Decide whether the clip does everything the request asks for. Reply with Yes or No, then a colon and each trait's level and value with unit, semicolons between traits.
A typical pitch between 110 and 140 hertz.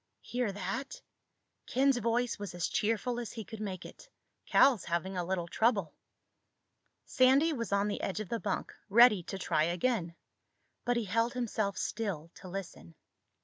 No: high, 210 Hz